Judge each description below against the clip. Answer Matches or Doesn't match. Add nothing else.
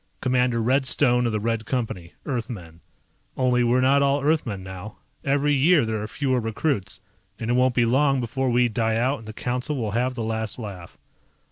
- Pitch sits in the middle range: Doesn't match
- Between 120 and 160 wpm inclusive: Doesn't match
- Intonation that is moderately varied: Matches